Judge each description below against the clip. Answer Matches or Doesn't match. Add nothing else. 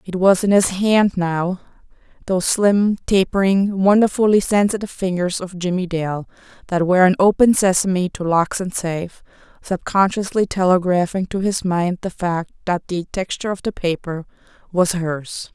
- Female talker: Matches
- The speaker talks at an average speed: Matches